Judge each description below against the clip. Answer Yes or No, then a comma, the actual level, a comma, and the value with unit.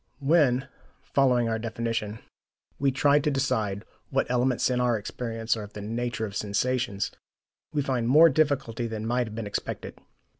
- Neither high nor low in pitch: No, low, 120 Hz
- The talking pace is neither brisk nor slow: Yes, average, 160 wpm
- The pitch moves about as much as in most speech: Yes, average, 3.1 semitones